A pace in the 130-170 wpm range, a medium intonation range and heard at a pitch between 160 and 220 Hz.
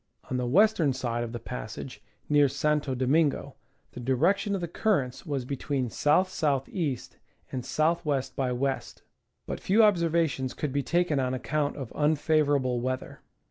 No: average, 160 wpm; average, 3.7 semitones; medium, 140 Hz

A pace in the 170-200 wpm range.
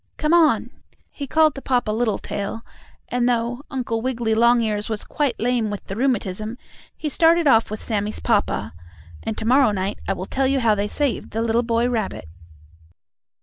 Yes: average, 175 wpm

